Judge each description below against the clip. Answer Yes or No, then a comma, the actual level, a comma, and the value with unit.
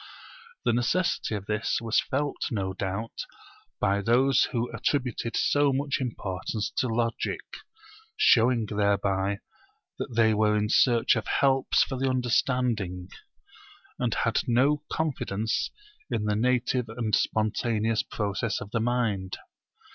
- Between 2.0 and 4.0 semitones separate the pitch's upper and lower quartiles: Yes, average, 3.2 semitones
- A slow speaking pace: Yes, slow, 125 wpm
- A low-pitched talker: Yes, low, 115 Hz